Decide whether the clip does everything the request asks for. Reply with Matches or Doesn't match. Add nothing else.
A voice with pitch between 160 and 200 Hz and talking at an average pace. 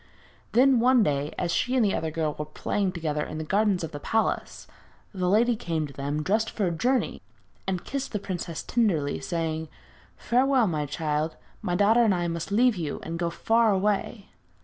Matches